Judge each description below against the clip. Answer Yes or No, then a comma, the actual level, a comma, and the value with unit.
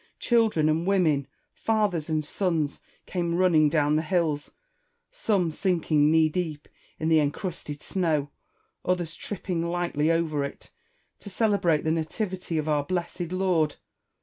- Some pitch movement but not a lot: Yes, average, 3.1 semitones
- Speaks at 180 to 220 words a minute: No, average, 150 wpm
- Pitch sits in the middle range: Yes, medium, 165 Hz